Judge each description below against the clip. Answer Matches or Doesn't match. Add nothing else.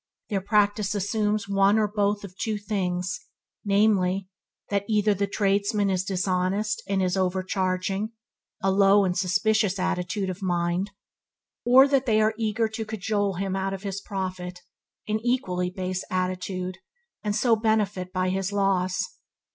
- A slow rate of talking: Doesn't match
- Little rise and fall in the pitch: Matches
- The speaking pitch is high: Matches